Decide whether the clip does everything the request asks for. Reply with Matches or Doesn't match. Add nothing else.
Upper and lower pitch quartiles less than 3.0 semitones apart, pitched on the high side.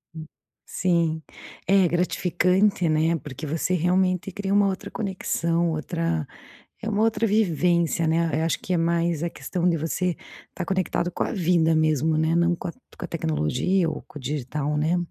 Doesn't match